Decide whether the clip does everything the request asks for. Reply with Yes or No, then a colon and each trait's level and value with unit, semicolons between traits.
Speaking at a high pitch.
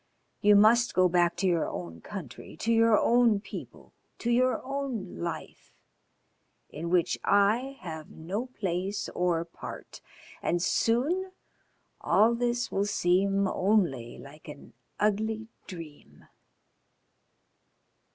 Yes: high, 200 Hz